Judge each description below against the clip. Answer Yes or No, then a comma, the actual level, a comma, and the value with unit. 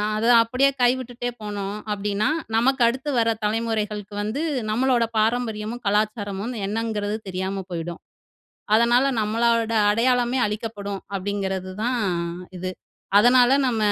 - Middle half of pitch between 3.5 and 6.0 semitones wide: No, average, 2.8 semitones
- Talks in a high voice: Yes, high, 220 Hz